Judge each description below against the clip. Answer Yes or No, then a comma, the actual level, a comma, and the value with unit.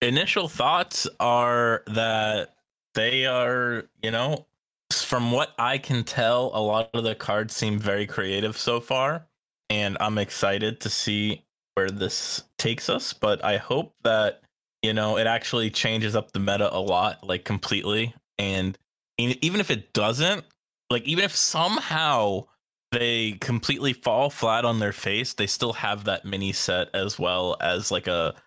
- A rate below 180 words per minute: Yes, average, 160 wpm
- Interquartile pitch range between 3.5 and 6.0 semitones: No, average, 3.1 semitones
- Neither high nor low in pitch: No, low, 110 Hz